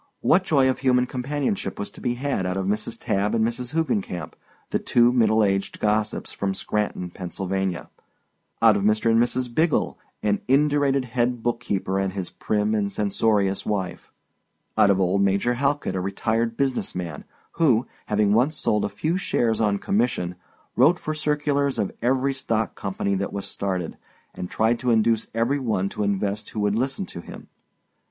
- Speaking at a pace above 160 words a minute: Yes, average, 170 wpm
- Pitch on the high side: No, low, 110 Hz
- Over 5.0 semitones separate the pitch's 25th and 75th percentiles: No, average, 4.7 semitones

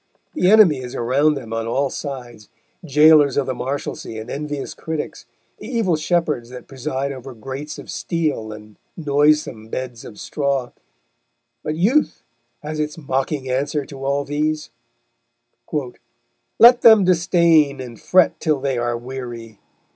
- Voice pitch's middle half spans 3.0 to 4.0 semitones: Yes, average, 3.6 semitones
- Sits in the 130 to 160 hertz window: Yes, medium, 140 Hz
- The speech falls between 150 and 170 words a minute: No, average, 140 wpm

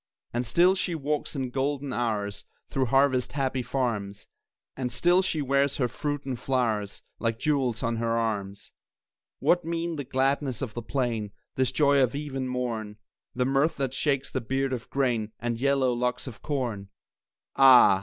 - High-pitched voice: No, low, 130 Hz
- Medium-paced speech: Yes, average, 170 wpm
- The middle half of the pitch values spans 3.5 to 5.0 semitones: No, average, 3.1 semitones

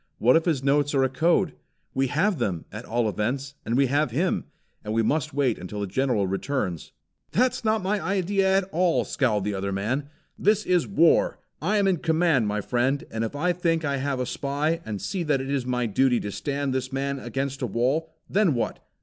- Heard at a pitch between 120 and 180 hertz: Yes, medium, 140 Hz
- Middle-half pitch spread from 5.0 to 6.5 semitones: Yes, wide, 5.5 semitones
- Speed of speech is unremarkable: No, fast, 220 wpm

